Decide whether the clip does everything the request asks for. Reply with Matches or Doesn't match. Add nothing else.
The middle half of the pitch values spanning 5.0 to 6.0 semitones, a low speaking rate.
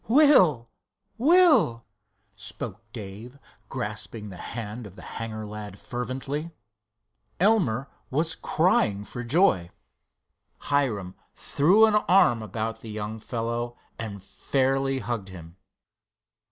Matches